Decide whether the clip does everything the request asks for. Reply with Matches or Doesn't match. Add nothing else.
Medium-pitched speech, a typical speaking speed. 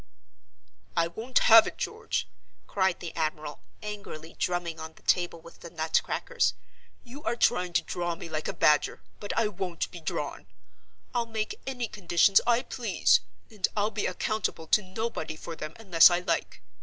Matches